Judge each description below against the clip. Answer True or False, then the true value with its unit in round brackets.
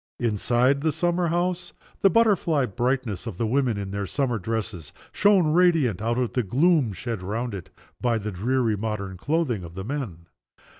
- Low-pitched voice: True (120 Hz)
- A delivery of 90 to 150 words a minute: False (170 wpm)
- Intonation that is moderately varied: False (6.4 semitones)